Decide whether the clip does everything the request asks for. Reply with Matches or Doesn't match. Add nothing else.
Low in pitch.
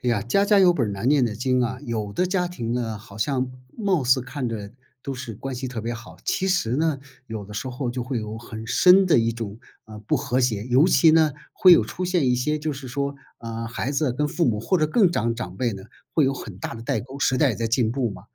Matches